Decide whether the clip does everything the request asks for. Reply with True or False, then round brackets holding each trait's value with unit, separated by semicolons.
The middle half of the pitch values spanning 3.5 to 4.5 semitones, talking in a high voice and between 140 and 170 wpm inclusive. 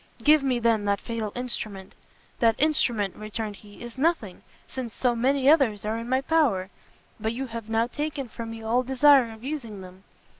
False (3.8 semitones; 235 Hz; 185 wpm)